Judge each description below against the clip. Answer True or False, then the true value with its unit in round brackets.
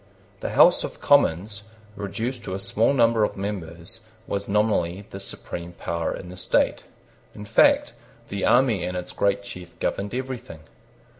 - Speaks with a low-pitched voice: True (100 Hz)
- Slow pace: False (155 wpm)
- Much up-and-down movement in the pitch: False (3.6 semitones)